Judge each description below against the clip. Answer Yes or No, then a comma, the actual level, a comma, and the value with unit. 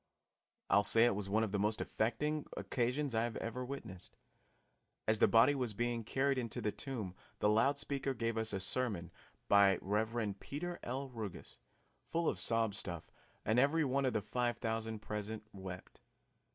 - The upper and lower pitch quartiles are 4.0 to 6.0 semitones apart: No, average, 3.6 semitones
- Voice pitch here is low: Yes, low, 115 Hz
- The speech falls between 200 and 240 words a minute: No, average, 175 wpm